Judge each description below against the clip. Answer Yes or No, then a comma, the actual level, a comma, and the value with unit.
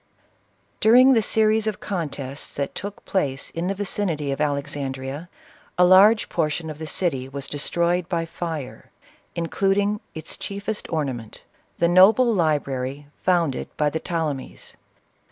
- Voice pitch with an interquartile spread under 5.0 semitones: No, average, 5.3 semitones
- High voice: No, medium, 165 Hz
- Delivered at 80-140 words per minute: Yes, slow, 135 wpm